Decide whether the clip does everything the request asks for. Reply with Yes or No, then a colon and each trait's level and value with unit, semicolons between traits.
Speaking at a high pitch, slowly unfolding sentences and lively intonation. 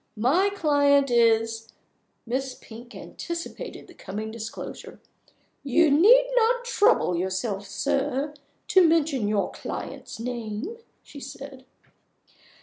Yes: very high, 270 Hz; slow, 110 wpm; wide, 6.7 semitones